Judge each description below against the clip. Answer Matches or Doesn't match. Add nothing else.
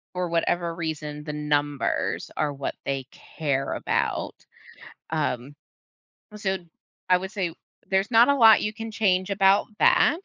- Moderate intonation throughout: Matches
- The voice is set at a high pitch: Doesn't match